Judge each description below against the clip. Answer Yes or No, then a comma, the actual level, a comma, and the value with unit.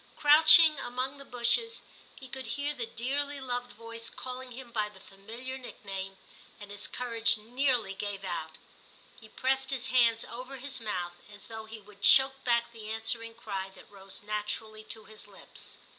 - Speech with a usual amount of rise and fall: Yes, average, 3.7 semitones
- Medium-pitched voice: No, high, 230 Hz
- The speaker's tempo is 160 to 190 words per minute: Yes, average, 170 wpm